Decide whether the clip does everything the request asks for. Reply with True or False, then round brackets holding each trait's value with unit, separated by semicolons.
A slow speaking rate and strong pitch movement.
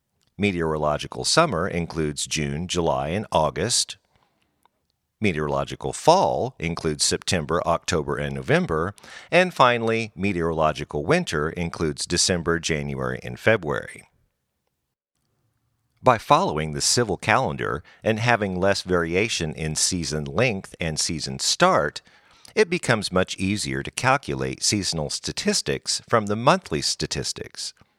True (105 wpm; 5.8 semitones)